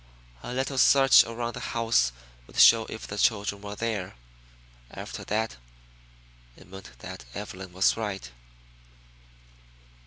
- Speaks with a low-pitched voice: Yes, low, 105 Hz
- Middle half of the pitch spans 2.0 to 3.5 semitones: Yes, average, 3.2 semitones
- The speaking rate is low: Yes, slow, 125 wpm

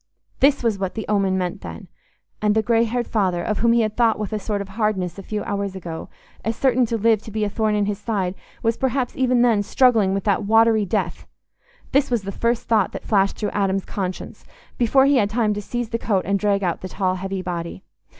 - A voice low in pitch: No, high, 210 Hz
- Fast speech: Yes, fast, 235 wpm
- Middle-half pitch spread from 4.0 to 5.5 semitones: No, average, 3.0 semitones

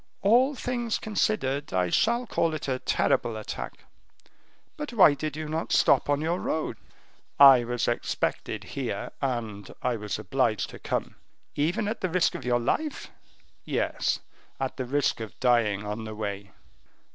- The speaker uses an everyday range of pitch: No, wide, 7.9 semitones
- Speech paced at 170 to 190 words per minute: No, average, 160 wpm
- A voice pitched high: No, low, 135 Hz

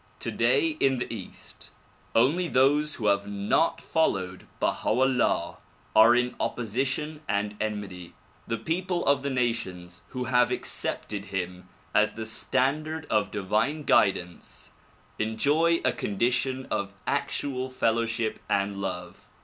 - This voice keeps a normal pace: No, slow, 125 wpm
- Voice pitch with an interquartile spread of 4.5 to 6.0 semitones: Yes, average, 5.2 semitones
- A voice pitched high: No, low, 115 Hz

